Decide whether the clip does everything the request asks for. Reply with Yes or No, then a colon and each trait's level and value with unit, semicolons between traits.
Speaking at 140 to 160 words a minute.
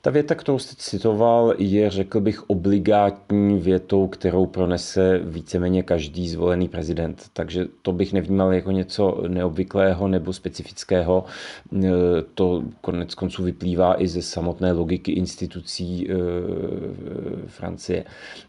No: slow, 115 wpm